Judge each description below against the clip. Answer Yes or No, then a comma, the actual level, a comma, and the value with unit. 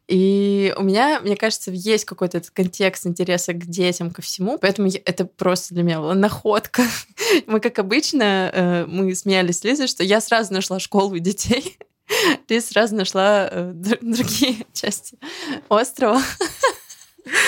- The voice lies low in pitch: No, high, 200 Hz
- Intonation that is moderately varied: Yes, average, 4.0 semitones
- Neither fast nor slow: Yes, average, 135 wpm